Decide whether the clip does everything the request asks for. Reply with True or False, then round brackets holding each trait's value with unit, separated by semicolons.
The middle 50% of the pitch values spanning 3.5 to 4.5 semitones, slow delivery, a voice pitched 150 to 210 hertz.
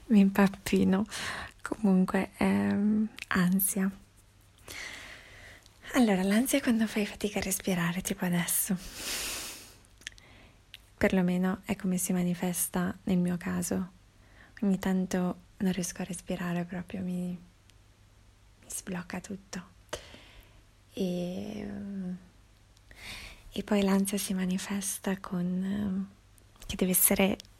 False (2.4 semitones; 95 wpm; 185 Hz)